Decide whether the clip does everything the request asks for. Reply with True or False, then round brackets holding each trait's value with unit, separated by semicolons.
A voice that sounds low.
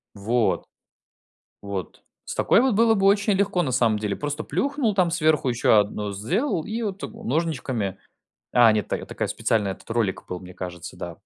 True (130 Hz)